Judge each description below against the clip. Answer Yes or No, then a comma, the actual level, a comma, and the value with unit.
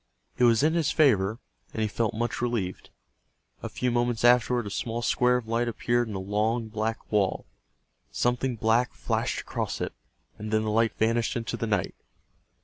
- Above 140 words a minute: Yes, average, 180 wpm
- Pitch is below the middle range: Yes, low, 115 Hz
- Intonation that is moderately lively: No, narrow, 2.0 semitones